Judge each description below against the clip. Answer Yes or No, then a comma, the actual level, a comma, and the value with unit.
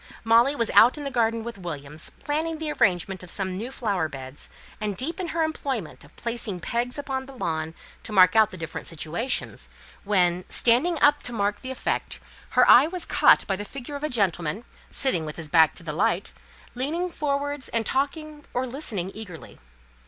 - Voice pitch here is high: Yes, high, 230 Hz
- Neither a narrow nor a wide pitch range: No, wide, 7.5 semitones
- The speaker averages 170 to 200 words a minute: Yes, average, 190 wpm